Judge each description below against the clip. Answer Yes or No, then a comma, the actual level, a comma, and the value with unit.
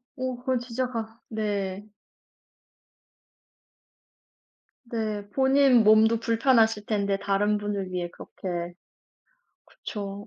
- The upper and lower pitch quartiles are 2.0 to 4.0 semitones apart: Yes, average, 2.8 semitones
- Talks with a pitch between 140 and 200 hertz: No, high, 215 Hz